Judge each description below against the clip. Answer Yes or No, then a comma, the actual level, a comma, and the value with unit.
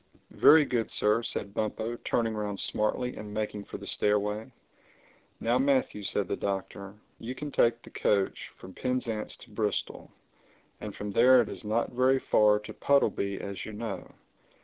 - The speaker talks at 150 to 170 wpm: Yes, average, 165 wpm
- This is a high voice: No, low, 110 Hz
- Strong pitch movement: No, average, 3.0 semitones